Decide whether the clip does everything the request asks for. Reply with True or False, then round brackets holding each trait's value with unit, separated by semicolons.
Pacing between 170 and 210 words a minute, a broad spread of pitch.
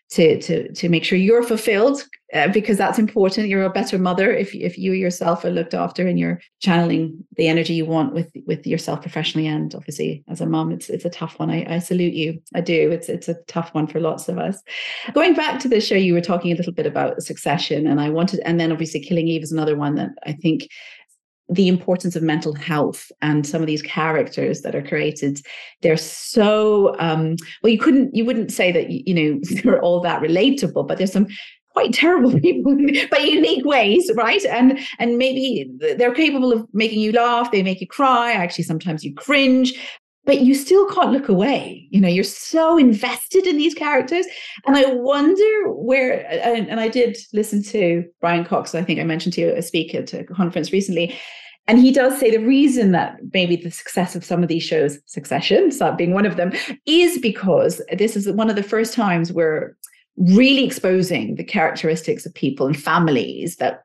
True (205 wpm; 7.1 semitones)